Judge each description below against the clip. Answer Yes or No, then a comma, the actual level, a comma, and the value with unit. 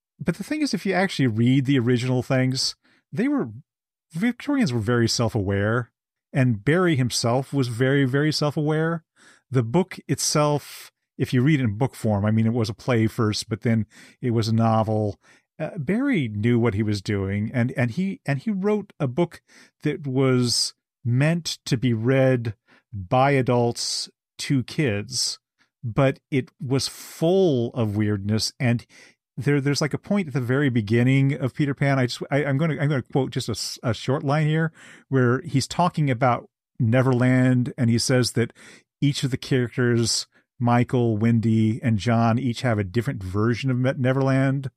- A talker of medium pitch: No, low, 130 Hz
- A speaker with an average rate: Yes, average, 175 wpm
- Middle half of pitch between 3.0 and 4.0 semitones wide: Yes, average, 3.5 semitones